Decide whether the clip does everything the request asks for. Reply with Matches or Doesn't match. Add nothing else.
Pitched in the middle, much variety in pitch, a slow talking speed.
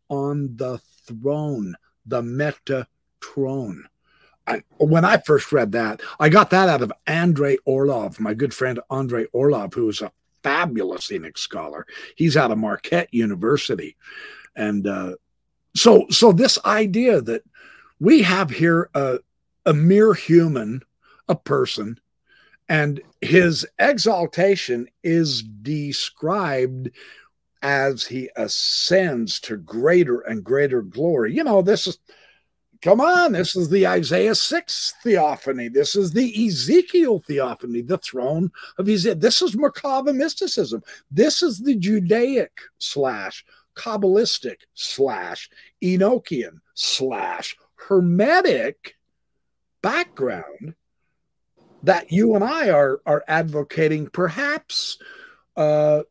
Matches